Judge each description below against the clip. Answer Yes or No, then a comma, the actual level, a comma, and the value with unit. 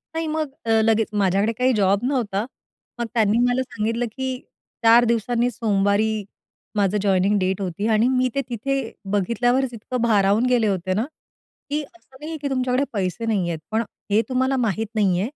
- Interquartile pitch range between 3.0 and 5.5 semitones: Yes, average, 3.7 semitones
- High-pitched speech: Yes, high, 225 Hz